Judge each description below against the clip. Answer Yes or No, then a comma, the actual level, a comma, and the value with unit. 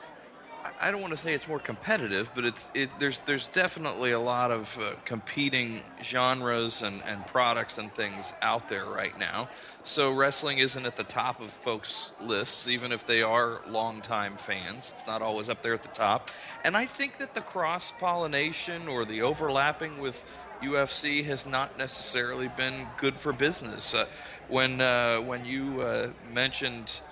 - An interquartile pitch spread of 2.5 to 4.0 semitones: Yes, average, 3.4 semitones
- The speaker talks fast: No, average, 175 wpm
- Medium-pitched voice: No, low, 130 Hz